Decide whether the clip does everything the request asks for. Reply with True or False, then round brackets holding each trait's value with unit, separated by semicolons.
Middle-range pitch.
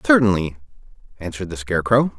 False (100 Hz)